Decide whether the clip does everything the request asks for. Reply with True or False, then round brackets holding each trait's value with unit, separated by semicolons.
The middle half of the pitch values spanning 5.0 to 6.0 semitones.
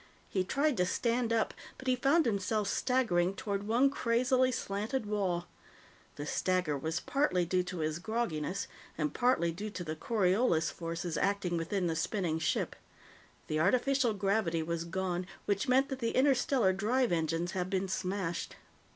True (5.5 semitones)